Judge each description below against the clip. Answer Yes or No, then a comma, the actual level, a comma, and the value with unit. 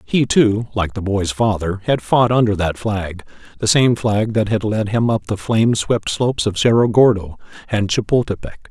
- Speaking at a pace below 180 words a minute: No, average, 195 wpm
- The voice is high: No, low, 110 Hz